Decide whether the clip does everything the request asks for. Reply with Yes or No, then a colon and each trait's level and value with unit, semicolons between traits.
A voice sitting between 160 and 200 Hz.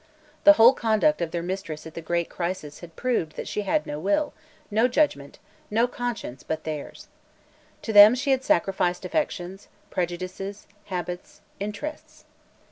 Yes: high, 190 Hz